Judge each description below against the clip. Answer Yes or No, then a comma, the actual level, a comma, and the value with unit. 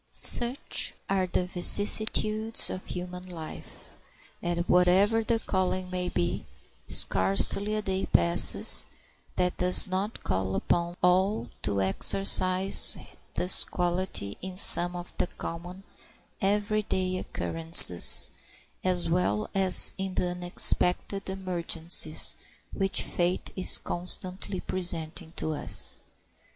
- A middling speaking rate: No, slow, 110 wpm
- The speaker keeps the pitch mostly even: Yes, narrow, 1.8 semitones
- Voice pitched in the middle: Yes, medium, 180 Hz